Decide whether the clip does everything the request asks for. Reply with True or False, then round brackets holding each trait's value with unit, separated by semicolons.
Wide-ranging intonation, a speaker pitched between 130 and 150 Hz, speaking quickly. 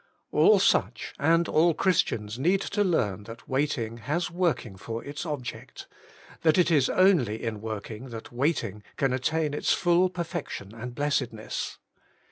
False (6.8 semitones; 135 Hz; 145 wpm)